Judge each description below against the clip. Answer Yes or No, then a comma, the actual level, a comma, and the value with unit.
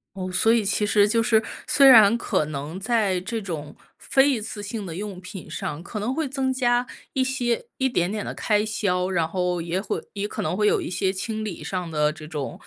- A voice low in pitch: No, high, 205 Hz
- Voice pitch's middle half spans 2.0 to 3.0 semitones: No, average, 4.2 semitones